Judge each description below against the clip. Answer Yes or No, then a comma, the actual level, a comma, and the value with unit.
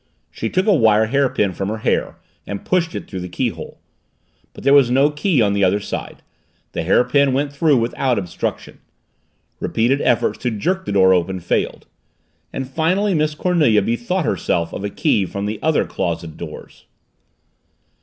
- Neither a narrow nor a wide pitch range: No, wide, 6.9 semitones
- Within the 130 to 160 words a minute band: No, average, 170 wpm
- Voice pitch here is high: No, low, 120 Hz